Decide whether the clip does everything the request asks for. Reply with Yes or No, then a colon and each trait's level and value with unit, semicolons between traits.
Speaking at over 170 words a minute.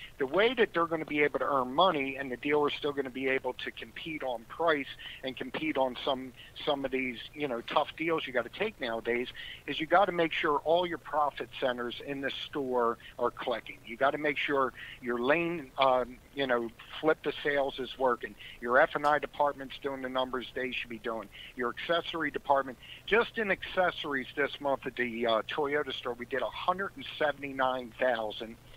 Yes: average, 200 wpm